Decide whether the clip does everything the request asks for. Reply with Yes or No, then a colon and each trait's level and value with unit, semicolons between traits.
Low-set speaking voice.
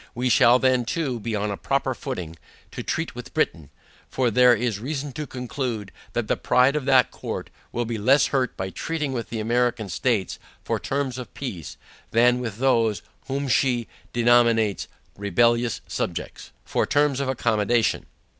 Yes: low, 120 Hz